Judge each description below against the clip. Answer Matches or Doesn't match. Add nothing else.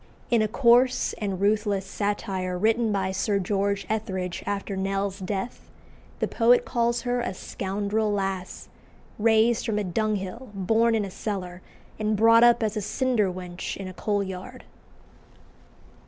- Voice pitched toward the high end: Matches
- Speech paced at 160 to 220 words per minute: Doesn't match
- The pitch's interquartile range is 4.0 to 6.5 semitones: Doesn't match